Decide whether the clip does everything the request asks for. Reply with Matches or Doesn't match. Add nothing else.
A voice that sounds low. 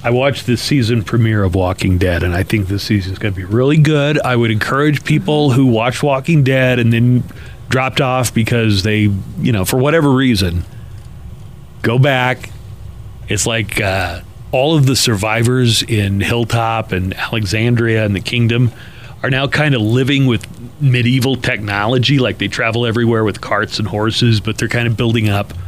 Matches